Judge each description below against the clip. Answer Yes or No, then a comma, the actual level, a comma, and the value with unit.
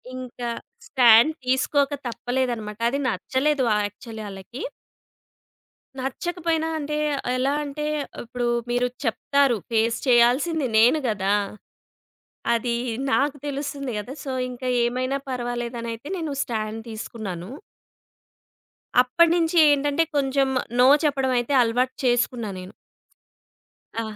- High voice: Yes, very high, 250 Hz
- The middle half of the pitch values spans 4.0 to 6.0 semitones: No, average, 3.3 semitones